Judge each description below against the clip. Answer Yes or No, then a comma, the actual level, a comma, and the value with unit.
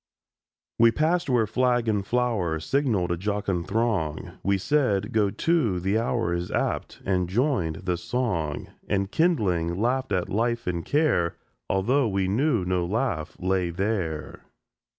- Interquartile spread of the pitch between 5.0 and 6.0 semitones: Yes, wide, 5.4 semitones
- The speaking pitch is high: No, low, 100 Hz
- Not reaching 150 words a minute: Yes, average, 140 wpm